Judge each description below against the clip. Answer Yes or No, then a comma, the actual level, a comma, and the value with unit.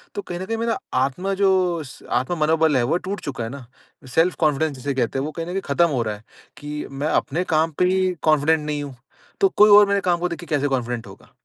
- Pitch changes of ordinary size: Yes, average, 4.9 semitones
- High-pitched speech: No, medium, 155 Hz